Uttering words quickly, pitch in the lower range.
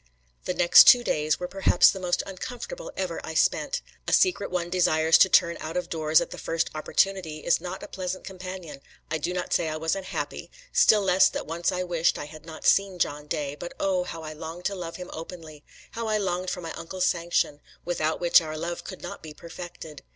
No: fast, 215 wpm; medium, 175 Hz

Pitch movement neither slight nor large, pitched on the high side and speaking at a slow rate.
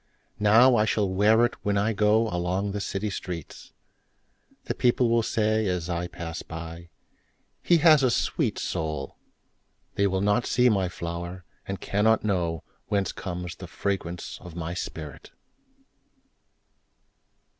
No: average, 3.8 semitones; very low, 95 Hz; slow, 115 wpm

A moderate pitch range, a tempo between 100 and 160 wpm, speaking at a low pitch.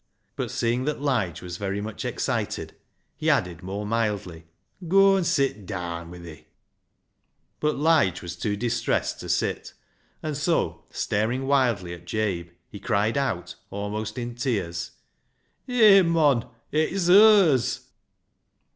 No: wide, 8.1 semitones; average, 145 wpm; low, 115 Hz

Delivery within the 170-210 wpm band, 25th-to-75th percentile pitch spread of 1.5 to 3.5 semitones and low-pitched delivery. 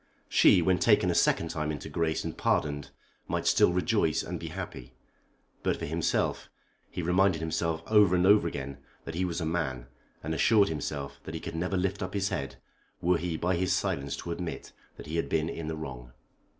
Yes: average, 200 wpm; average, 3.0 semitones; very low, 85 Hz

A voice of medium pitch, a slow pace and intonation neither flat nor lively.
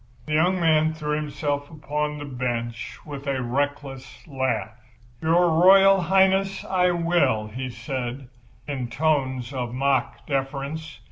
Yes: medium, 145 Hz; slow, 130 wpm; average, 3.6 semitones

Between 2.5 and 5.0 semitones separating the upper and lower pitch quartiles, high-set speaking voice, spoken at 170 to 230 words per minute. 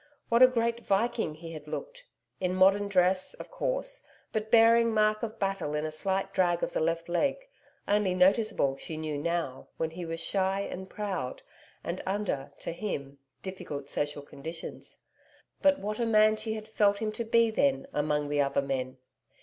No: wide, 5.6 semitones; high, 195 Hz; average, 180 wpm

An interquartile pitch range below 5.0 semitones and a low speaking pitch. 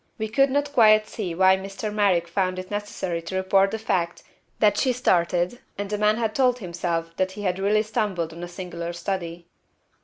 No: average, 3.5 semitones; high, 190 Hz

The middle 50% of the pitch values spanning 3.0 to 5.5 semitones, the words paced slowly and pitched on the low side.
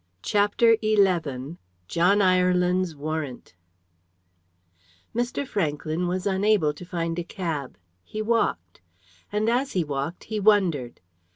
No: average, 4.9 semitones; slow, 110 wpm; medium, 180 Hz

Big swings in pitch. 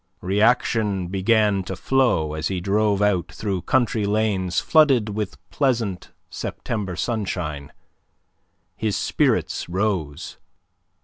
No: average, 3.1 semitones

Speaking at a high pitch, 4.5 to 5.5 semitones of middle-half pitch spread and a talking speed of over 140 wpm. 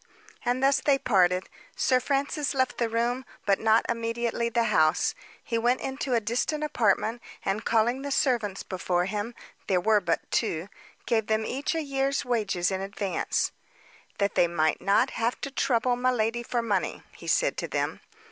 No: high, 230 Hz; average, 4.1 semitones; average, 170 wpm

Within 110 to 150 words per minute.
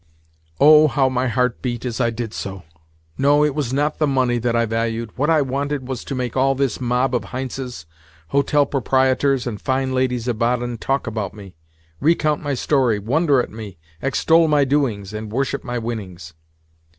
No: average, 180 wpm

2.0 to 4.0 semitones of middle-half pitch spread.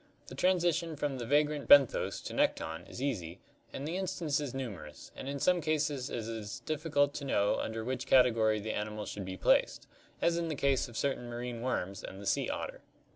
No: average, 5.2 semitones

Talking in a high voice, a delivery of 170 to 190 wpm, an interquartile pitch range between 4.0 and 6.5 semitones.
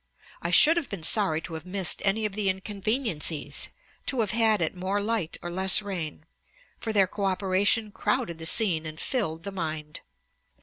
Yes: high, 195 Hz; average, 175 wpm; average, 4.4 semitones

